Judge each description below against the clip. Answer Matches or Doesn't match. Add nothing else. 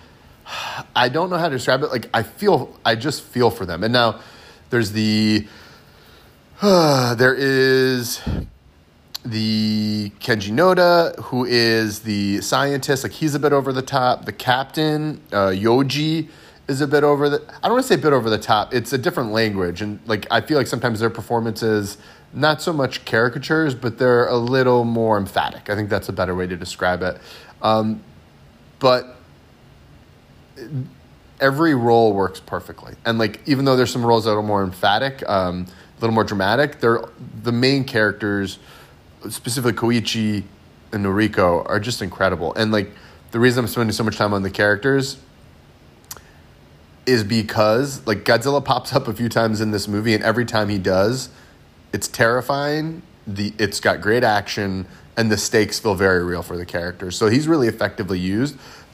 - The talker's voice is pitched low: Matches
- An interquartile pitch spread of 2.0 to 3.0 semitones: Doesn't match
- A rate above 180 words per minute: Doesn't match